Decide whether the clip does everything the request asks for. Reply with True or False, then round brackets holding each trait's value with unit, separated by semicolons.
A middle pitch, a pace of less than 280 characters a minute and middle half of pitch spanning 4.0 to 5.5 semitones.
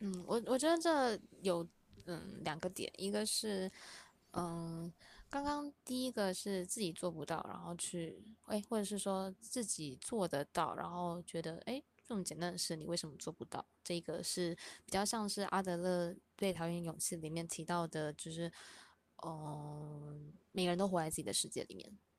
False (175 Hz; 250 characters per minute; 3.5 semitones)